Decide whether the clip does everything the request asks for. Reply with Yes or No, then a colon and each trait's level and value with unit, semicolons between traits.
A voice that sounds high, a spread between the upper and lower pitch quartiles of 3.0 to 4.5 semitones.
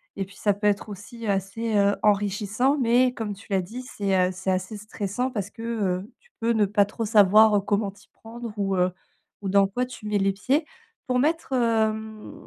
No: high, 210 Hz; narrow, 2.6 semitones